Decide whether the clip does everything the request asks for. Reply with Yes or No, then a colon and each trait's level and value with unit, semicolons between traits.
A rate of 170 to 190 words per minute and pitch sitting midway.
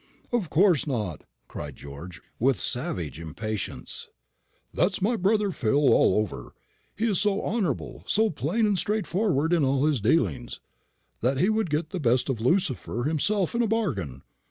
No: average, 155 wpm; medium, 150 Hz